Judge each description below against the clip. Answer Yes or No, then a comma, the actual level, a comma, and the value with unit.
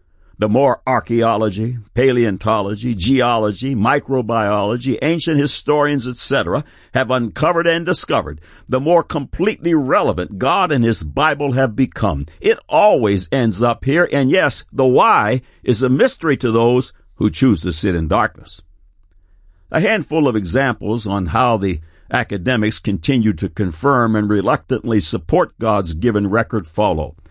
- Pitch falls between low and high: No, low, 115 Hz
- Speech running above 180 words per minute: No, slow, 135 wpm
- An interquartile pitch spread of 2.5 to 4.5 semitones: No, average, 5.0 semitones